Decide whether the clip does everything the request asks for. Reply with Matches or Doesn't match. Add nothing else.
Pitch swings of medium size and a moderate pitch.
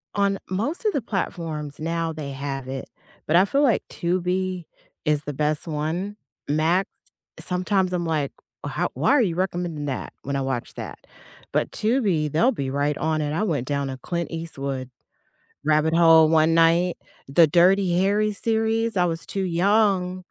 Matches